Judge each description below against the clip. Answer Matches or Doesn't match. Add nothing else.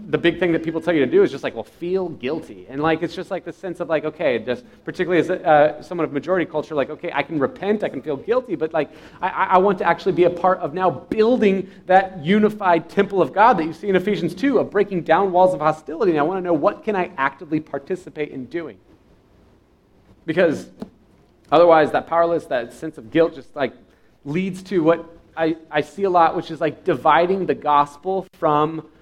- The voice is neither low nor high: Matches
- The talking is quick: Matches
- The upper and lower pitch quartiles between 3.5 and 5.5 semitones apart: Doesn't match